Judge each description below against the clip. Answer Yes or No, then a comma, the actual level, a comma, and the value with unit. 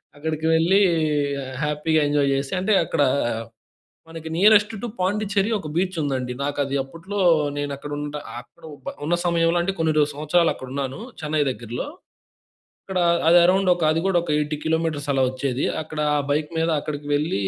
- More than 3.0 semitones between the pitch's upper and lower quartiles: Yes, average, 3.4 semitones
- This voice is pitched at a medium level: Yes, medium, 155 Hz